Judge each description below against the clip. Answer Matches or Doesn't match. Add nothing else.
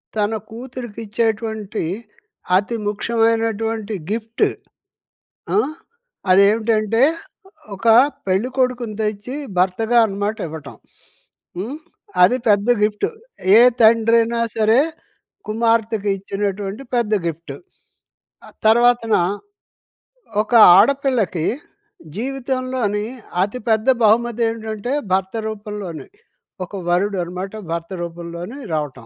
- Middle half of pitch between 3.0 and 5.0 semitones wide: Doesn't match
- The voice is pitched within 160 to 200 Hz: Doesn't match